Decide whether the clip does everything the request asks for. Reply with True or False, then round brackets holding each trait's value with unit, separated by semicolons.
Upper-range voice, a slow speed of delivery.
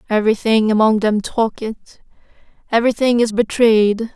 True (220 Hz; 100 wpm)